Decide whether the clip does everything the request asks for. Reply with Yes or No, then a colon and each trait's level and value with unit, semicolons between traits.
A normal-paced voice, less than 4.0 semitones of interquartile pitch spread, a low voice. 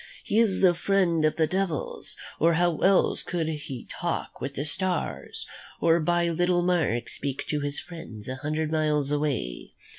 No: average, 170 wpm; average, 3.2 semitones; medium, 160 Hz